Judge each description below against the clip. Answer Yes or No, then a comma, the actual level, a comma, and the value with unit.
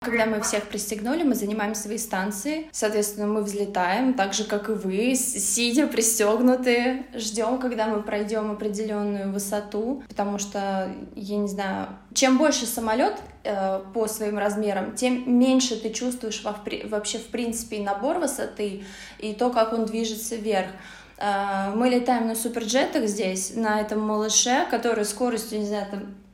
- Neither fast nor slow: Yes, average, 150 wpm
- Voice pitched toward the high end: Yes, high, 215 Hz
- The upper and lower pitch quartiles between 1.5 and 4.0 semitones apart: Yes, narrow, 2.5 semitones